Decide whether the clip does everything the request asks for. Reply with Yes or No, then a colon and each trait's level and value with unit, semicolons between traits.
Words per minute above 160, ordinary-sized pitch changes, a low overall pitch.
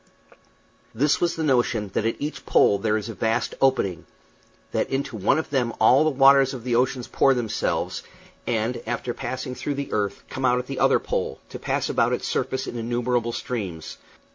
Yes: average, 190 wpm; average, 3.1 semitones; low, 125 Hz